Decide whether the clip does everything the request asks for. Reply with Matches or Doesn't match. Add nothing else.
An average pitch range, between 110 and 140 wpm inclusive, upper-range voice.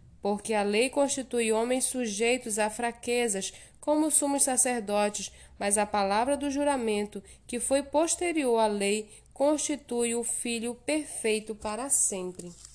Matches